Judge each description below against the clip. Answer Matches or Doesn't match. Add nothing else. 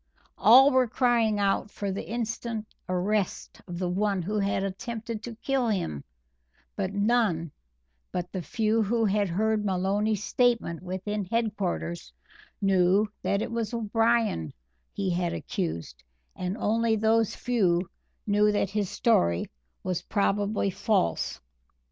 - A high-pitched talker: Matches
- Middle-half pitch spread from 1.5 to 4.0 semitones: Matches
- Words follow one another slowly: Matches